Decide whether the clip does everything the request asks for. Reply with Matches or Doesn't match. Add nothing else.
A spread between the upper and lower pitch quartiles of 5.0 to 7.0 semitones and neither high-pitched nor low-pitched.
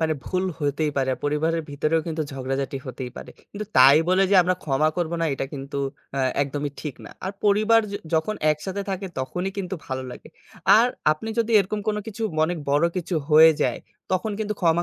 Matches